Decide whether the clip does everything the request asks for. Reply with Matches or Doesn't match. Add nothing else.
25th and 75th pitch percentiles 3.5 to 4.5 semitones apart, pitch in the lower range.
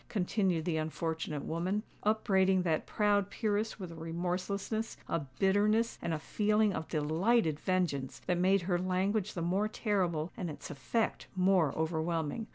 Doesn't match